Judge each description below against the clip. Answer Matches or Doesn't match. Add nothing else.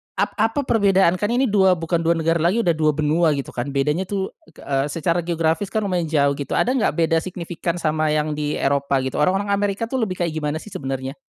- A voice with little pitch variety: Doesn't match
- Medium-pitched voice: Matches